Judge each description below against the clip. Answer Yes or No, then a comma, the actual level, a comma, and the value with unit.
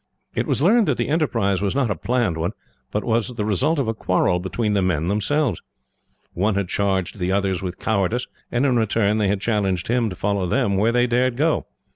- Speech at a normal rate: No, fast, 215 wpm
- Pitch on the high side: No, low, 105 Hz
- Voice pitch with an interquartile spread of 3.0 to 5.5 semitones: Yes, average, 4.2 semitones